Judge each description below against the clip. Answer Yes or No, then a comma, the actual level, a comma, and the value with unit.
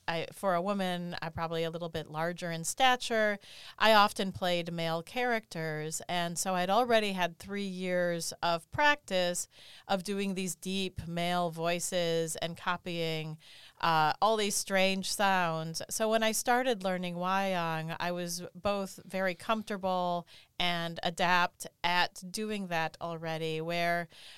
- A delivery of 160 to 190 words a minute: No, average, 140 wpm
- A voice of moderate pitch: Yes, medium, 175 Hz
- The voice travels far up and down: No, average, 2.7 semitones